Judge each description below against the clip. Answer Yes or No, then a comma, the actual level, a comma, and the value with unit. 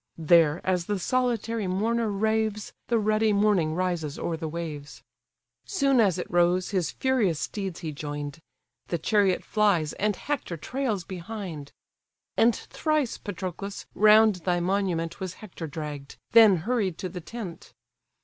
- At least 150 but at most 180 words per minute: No, average, 140 wpm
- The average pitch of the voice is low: No, high, 190 Hz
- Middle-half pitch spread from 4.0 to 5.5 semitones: Yes, average, 4.4 semitones